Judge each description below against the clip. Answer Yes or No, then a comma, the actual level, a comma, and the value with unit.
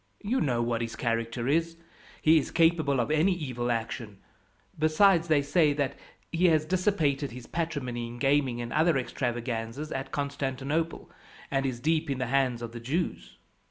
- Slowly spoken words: No, average, 165 wpm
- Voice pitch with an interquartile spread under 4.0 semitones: No, average, 4.8 semitones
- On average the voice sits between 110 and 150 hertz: Yes, medium, 140 Hz